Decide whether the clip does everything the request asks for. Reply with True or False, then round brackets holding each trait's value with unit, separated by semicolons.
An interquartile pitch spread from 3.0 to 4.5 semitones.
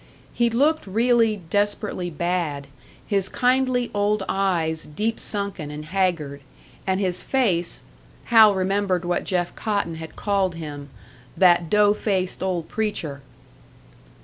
True (3.6 semitones)